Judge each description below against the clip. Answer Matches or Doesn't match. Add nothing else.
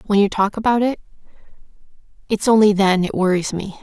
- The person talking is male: Doesn't match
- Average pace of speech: Matches